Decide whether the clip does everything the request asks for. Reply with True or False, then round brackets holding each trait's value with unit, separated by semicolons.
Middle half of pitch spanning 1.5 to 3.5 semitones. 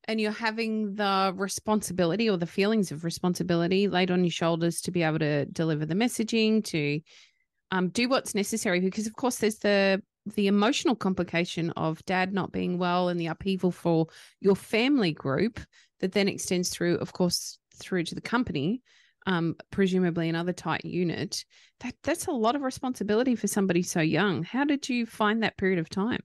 False (4.1 semitones)